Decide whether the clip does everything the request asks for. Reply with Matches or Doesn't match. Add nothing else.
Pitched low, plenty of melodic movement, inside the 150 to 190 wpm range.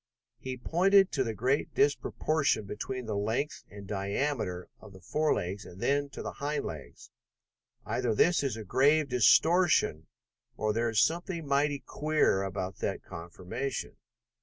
Doesn't match